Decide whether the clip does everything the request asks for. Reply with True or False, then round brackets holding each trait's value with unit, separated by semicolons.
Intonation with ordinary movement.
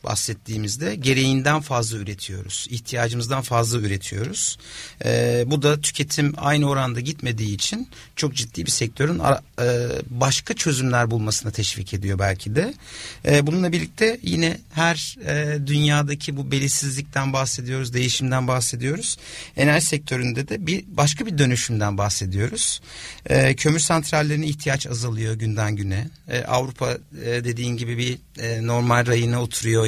True (4.1 semitones)